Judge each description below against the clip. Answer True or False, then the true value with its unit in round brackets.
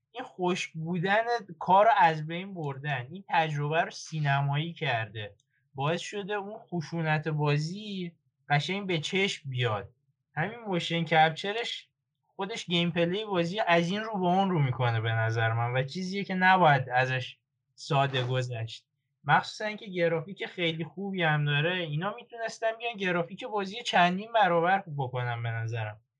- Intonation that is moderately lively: False (5.8 semitones)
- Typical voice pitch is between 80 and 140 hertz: False (165 Hz)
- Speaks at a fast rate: False (140 wpm)